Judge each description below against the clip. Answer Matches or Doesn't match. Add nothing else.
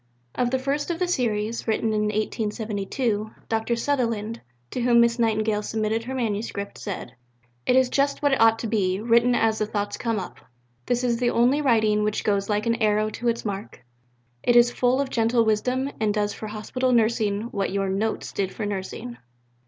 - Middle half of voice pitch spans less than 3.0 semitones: Matches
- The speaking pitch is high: Matches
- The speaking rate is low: Doesn't match